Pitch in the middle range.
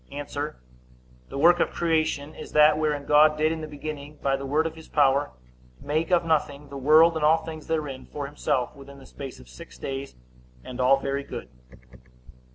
Yes: medium, 150 Hz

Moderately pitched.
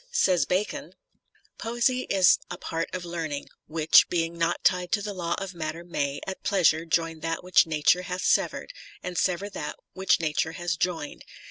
Yes: medium, 175 Hz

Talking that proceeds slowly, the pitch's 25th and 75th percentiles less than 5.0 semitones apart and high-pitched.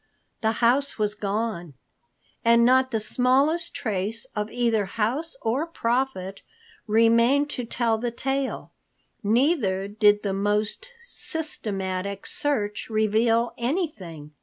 Yes: slow, 110 wpm; average, 4.0 semitones; high, 230 Hz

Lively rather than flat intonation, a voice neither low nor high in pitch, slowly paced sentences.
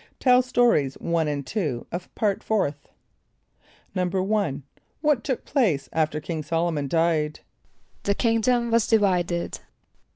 Yes: wide, 6.8 semitones; medium, 180 Hz; slow, 125 wpm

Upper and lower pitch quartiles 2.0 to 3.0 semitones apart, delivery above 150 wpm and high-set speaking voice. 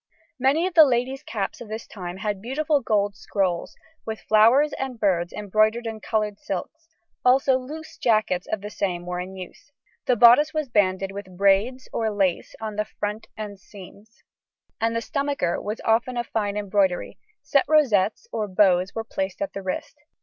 No: average, 4.4 semitones; average, 175 wpm; high, 215 Hz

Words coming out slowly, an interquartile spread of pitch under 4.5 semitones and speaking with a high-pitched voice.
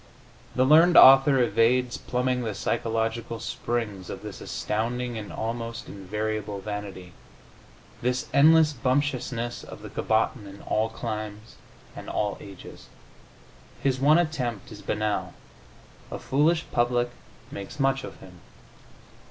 No: slow, 120 wpm; average, 3.3 semitones; low, 115 Hz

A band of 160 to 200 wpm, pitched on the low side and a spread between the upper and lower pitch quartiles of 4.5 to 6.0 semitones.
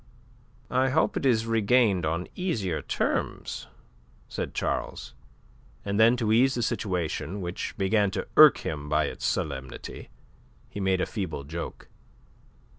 No: average, 145 wpm; low, 100 Hz; average, 5.1 semitones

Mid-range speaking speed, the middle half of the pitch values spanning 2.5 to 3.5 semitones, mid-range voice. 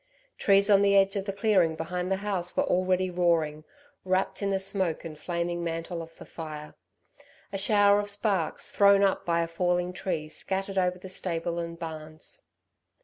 Yes: average, 180 wpm; average, 2.8 semitones; medium, 180 Hz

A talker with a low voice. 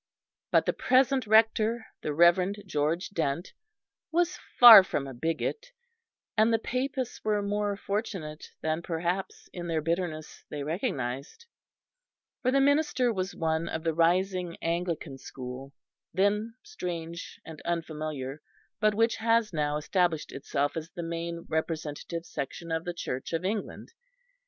No: medium, 175 Hz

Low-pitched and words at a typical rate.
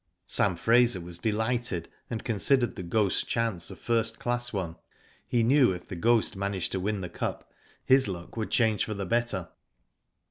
Yes: low, 110 Hz; average, 175 wpm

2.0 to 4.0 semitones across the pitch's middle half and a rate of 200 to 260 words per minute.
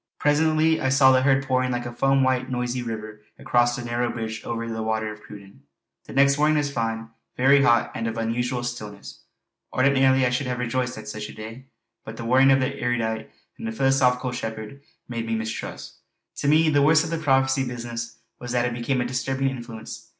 Yes: average, 2.7 semitones; fast, 205 wpm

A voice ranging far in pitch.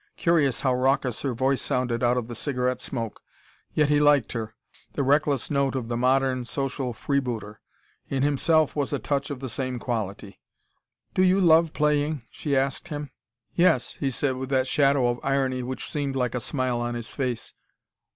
No: narrow, 2.6 semitones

